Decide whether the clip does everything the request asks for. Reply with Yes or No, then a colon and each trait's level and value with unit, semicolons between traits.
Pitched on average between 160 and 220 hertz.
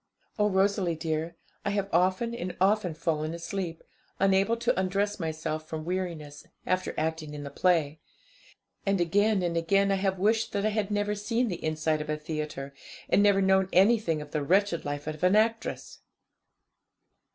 Yes: medium, 185 Hz